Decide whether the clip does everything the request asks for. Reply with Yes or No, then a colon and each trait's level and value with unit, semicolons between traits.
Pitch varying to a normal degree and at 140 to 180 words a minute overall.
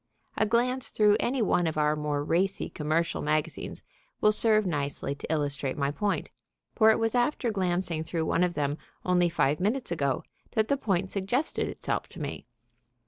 No: wide, 6.2 semitones; average, 175 wpm